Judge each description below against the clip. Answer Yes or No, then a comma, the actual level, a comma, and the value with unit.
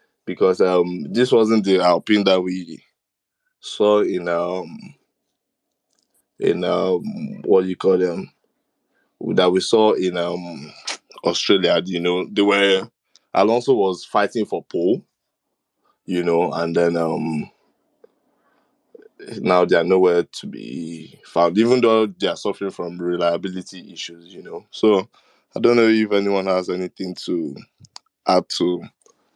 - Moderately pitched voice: No, very low, 90 Hz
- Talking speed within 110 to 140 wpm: Yes, slow, 135 wpm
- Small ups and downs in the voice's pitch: No, average, 3.1 semitones